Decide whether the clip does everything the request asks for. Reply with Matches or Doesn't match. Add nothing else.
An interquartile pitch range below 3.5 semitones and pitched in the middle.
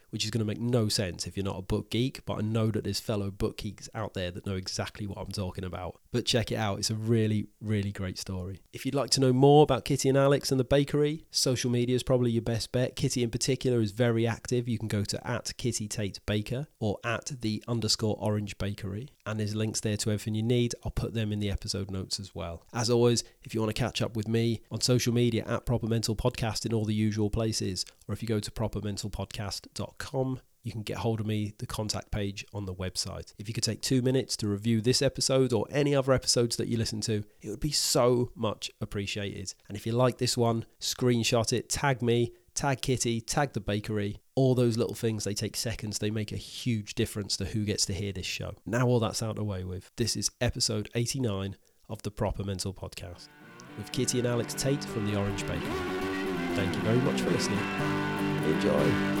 Doesn't match